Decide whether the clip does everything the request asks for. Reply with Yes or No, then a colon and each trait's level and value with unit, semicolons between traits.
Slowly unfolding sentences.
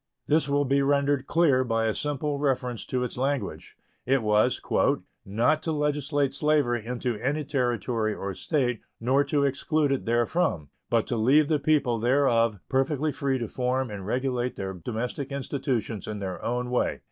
No: average, 165 wpm